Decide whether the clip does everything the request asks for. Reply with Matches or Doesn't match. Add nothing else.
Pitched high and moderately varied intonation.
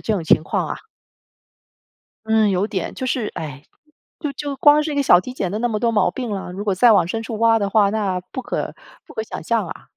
Matches